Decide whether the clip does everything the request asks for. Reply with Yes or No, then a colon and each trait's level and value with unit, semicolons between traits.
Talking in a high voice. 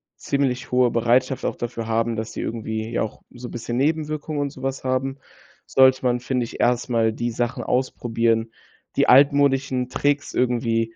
No: low, 125 Hz